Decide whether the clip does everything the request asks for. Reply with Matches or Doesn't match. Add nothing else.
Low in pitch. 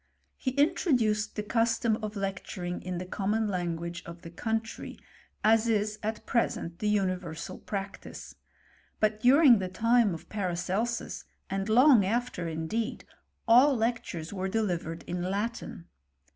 Doesn't match